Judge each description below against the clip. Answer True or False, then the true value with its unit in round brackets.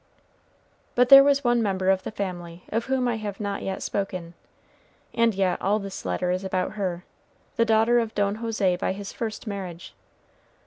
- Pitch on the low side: False (200 Hz)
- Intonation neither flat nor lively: True (3.4 semitones)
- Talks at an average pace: True (180 wpm)